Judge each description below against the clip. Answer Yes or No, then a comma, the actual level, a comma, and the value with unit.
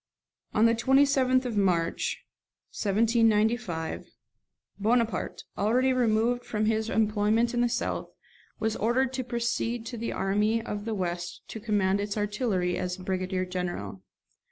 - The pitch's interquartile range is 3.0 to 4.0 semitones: Yes, average, 3.5 semitones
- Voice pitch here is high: Yes, high, 220 Hz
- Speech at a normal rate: No, slow, 130 wpm